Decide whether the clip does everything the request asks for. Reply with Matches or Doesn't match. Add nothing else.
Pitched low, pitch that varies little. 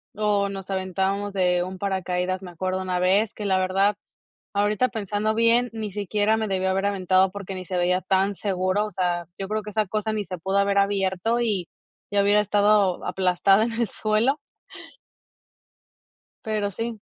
Doesn't match